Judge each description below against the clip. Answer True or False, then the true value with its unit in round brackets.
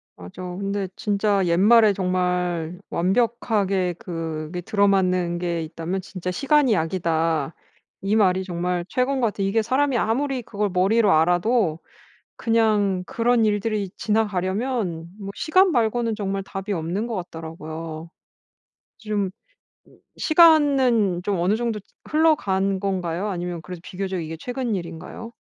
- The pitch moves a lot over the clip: False (4.1 semitones)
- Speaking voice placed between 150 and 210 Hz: True (195 Hz)